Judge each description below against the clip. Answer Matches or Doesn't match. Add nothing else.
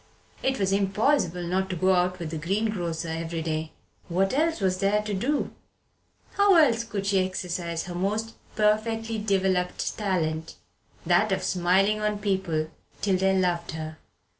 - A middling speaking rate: Matches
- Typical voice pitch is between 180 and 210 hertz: Matches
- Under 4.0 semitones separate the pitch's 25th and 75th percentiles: Matches